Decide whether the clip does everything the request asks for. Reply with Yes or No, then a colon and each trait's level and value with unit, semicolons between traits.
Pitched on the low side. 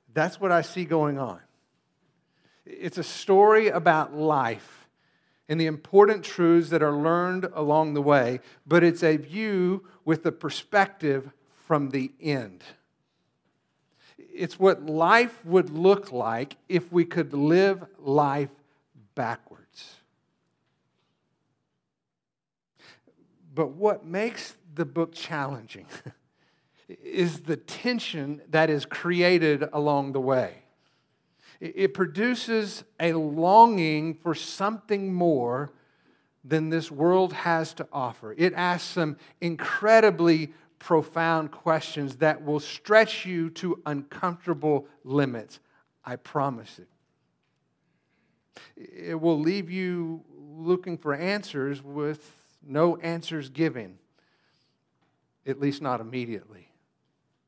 No: medium, 160 Hz